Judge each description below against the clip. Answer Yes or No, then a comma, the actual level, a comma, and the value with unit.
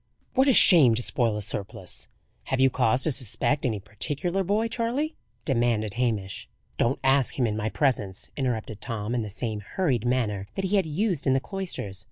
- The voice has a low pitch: Yes, low, 125 Hz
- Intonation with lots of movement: Yes, wide, 6.7 semitones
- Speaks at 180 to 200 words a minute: Yes, average, 190 wpm